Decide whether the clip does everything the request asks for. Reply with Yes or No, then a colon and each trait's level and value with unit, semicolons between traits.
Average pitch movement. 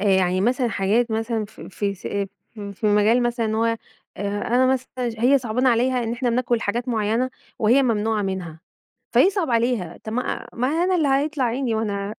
Yes: average, 3.2 semitones